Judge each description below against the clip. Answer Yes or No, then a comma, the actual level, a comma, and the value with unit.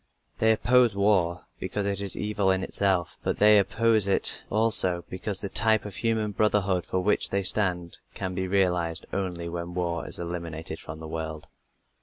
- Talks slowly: No, average, 175 wpm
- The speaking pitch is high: No, very low, 95 Hz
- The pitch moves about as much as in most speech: Yes, average, 3.2 semitones